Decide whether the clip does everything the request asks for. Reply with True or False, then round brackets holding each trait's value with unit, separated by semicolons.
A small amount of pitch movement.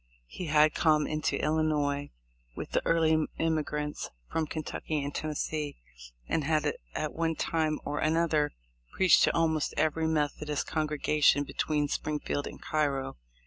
True (1.2 semitones)